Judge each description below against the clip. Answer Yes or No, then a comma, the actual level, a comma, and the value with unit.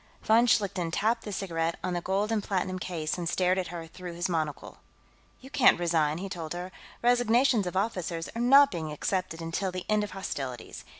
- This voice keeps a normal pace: Yes, average, 195 wpm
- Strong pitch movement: No, average, 3.9 semitones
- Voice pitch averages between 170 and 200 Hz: Yes, medium, 185 Hz